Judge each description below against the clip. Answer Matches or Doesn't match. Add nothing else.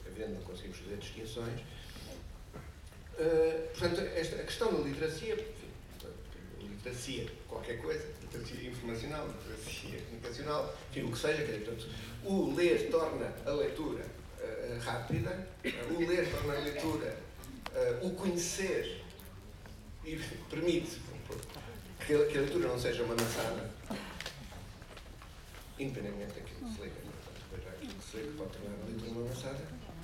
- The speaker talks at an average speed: Matches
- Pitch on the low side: Matches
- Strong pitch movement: Matches